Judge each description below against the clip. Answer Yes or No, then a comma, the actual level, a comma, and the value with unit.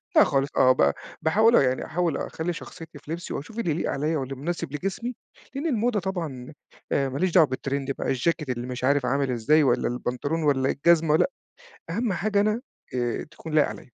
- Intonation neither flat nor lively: Yes, average, 4.8 semitones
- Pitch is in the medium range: Yes, medium, 155 Hz